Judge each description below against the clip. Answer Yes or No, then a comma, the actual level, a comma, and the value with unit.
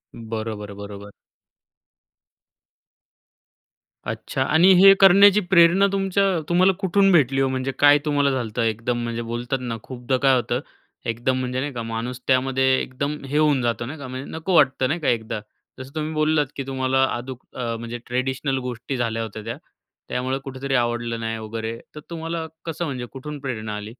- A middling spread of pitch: Yes, average, 4.2 semitones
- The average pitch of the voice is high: No, low, 130 Hz